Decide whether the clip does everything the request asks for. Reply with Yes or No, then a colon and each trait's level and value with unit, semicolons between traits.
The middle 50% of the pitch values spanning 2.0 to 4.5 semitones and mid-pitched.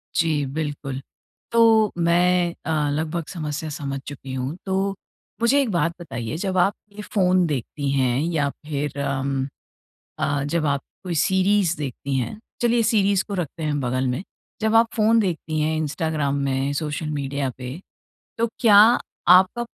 No: average, 5.2 semitones; medium, 155 Hz